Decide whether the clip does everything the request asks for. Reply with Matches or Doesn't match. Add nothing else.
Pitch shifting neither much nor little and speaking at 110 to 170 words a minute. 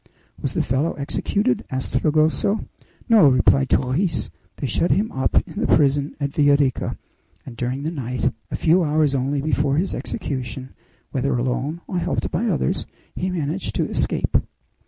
Matches